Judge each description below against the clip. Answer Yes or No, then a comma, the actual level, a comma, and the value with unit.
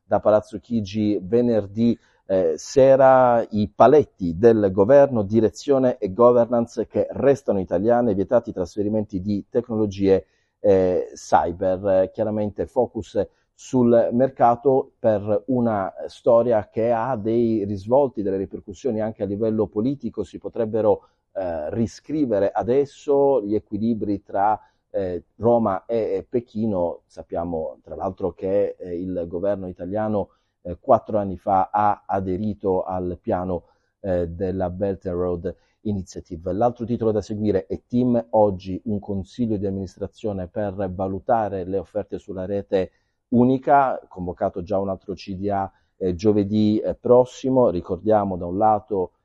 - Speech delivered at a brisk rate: No, average, 125 wpm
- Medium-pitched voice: No, low, 105 Hz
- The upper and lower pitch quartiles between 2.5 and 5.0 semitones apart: Yes, average, 3.5 semitones